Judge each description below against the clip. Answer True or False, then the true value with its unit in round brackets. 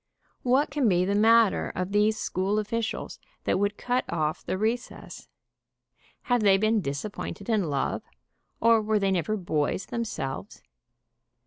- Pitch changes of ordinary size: True (3.4 semitones)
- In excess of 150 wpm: False (145 wpm)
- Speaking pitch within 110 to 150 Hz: False (210 Hz)